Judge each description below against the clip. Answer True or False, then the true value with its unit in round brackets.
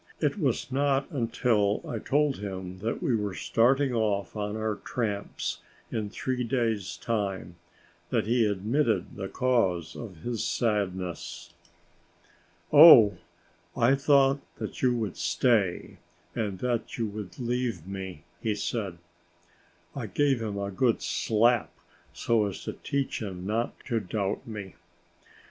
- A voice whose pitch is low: True (110 Hz)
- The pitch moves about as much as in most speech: True (4.0 semitones)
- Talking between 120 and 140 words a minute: True (135 wpm)